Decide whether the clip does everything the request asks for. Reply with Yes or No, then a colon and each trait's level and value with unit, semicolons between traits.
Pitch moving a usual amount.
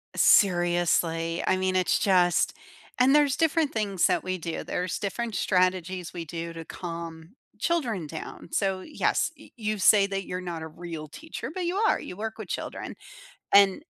Yes: average, 4.0 semitones